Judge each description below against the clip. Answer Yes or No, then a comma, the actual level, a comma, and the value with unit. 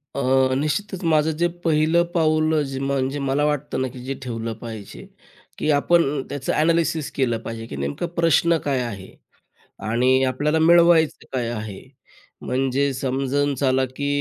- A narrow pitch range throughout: No, average, 3.4 semitones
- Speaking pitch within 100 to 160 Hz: Yes, medium, 140 Hz